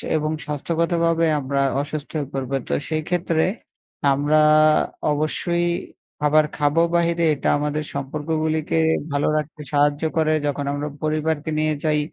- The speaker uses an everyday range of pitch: No, narrow, 1.7 semitones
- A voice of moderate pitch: Yes, medium, 155 Hz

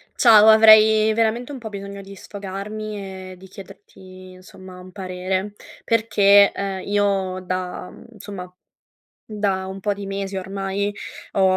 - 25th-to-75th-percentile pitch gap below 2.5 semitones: Yes, narrow, 1.9 semitones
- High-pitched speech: Yes, high, 195 Hz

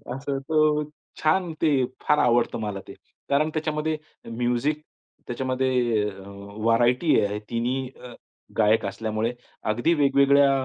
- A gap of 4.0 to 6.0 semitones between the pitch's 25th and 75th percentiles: Yes, average, 4.4 semitones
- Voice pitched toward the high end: No, low, 130 Hz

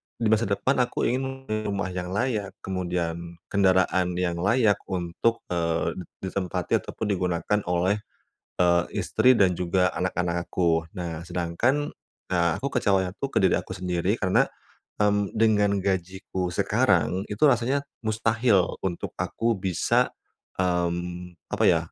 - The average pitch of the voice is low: Yes, very low, 95 Hz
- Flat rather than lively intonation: No, average, 3.2 semitones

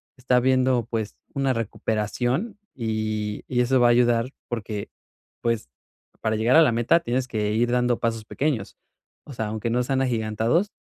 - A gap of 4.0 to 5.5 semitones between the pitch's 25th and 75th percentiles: No, average, 2.7 semitones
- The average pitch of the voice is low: Yes, low, 120 Hz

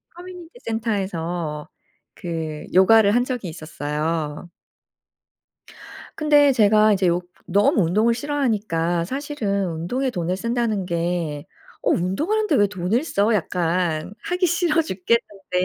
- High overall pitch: Yes, high, 200 Hz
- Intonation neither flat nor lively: No, wide, 6.3 semitones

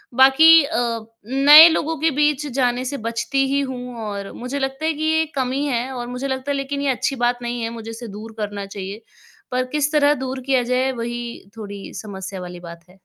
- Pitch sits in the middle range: No, very high, 255 Hz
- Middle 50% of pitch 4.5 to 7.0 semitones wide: No, average, 3.7 semitones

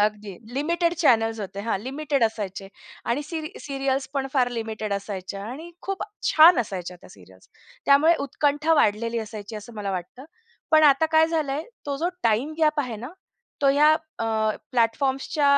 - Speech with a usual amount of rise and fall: No, wide, 6.0 semitones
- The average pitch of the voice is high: Yes, very high, 265 Hz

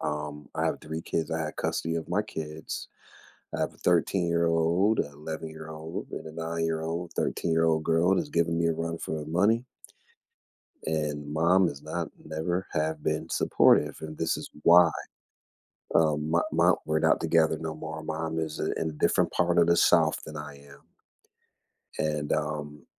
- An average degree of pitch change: No, narrow, 1.3 semitones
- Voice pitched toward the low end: Yes, very low, 80 Hz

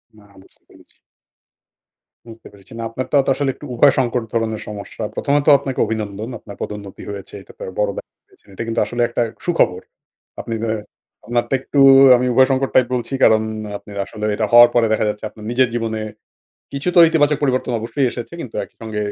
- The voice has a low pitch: Yes, low, 115 Hz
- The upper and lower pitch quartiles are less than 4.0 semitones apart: Yes, average, 3.2 semitones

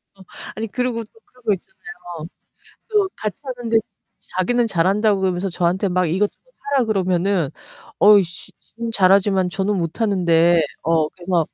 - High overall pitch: Yes, high, 195 Hz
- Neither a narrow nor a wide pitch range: Yes, average, 4.3 semitones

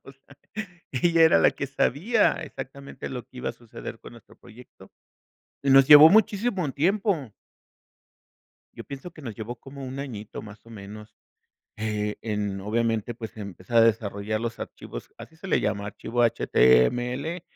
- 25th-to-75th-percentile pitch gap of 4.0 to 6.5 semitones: Yes, average, 4.8 semitones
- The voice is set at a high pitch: No, low, 120 Hz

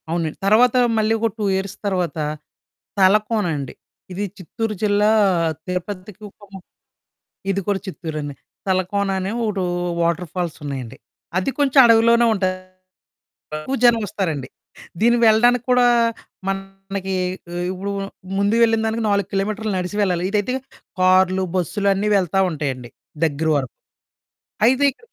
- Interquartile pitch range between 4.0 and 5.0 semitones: No, average, 3.3 semitones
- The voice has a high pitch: Yes, high, 195 Hz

